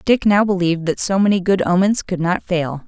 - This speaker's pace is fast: Yes, fast, 230 wpm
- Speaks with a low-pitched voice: No, medium, 185 Hz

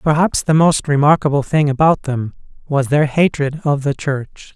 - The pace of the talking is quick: No, average, 170 wpm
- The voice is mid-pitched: Yes, medium, 145 Hz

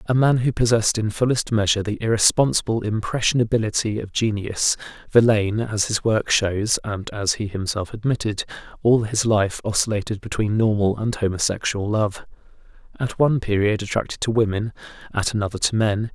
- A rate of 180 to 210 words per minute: No, average, 145 wpm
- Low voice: Yes, low, 110 Hz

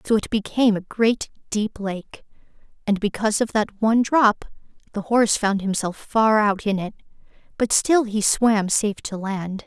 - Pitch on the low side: No, high, 210 Hz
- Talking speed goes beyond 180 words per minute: No, average, 175 wpm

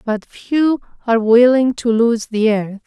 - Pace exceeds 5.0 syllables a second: No, 4.0 syllables/s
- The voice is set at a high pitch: Yes, high, 235 Hz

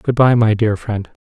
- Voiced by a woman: No, male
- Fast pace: Yes, fast, 245 wpm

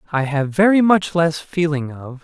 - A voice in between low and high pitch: Yes, medium, 160 Hz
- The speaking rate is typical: Yes, average, 190 wpm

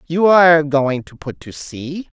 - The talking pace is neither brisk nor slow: Yes, average, 190 wpm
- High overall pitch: No, medium, 155 Hz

